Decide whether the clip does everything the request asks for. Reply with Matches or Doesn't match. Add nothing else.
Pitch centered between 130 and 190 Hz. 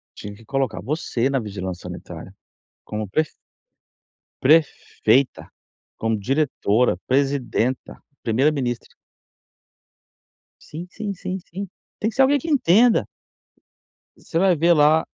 Matches